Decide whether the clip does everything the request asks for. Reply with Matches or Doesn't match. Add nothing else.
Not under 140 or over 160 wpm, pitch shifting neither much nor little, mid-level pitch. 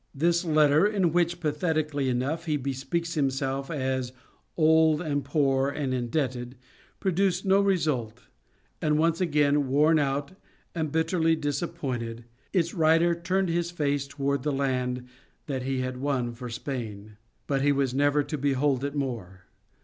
Matches